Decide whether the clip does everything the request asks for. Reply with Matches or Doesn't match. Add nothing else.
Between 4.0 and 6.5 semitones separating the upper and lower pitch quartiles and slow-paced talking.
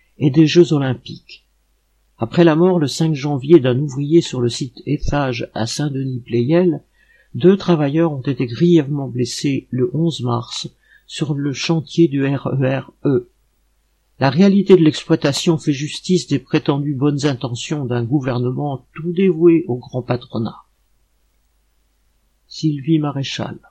Matches